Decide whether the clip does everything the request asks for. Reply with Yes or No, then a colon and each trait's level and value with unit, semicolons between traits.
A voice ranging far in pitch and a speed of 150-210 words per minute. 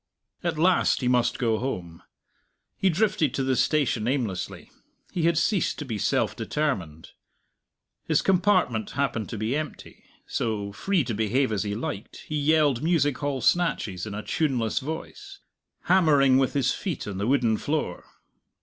Yes: wide, 6.1 semitones; average, 160 wpm